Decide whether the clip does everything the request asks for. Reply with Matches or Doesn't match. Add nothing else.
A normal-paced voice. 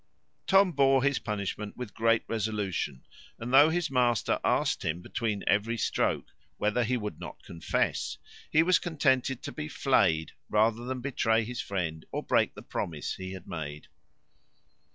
Matches